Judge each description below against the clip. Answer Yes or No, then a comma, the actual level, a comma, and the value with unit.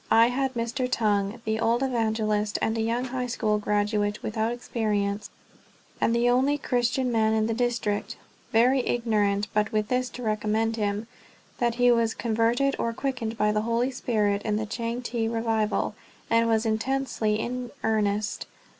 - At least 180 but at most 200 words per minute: No, average, 160 wpm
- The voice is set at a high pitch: Yes, high, 225 Hz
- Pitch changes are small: Yes, narrow, 2.3 semitones